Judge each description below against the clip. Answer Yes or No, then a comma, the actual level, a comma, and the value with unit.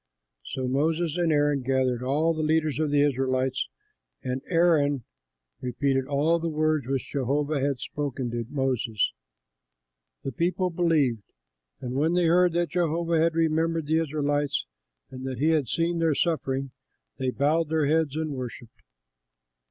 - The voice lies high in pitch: No, medium, 145 Hz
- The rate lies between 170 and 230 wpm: No, average, 150 wpm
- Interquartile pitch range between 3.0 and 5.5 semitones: Yes, average, 3.6 semitones